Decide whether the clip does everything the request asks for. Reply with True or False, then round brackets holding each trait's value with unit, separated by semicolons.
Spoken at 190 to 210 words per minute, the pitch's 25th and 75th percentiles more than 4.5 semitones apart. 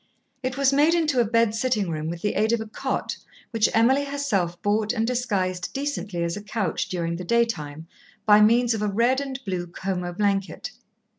True (195 wpm; 5.1 semitones)